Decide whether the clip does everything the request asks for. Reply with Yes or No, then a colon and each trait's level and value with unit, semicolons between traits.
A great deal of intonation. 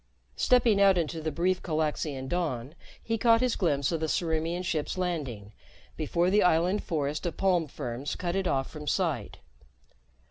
No: average, 3.7 semitones